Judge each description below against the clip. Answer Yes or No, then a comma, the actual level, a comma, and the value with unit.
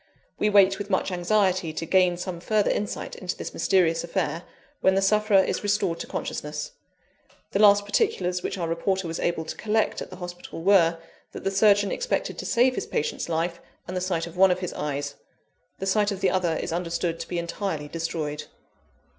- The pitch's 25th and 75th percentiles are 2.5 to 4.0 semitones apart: Yes, average, 3.1 semitones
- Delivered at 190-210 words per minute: Yes, average, 195 wpm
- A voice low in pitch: No, medium, 185 Hz